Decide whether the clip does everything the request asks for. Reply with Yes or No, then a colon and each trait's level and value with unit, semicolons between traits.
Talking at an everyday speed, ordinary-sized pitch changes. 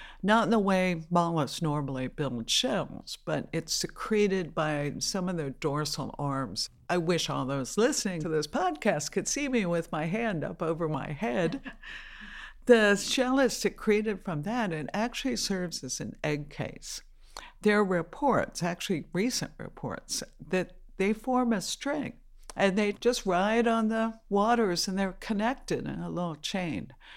No: average, 160 wpm; wide, 5.9 semitones